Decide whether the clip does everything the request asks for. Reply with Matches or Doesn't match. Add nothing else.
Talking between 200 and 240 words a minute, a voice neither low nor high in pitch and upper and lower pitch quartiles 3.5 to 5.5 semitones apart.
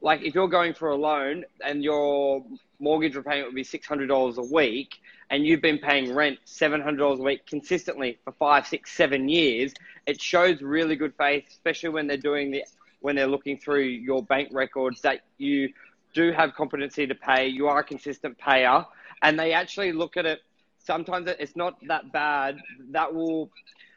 Doesn't match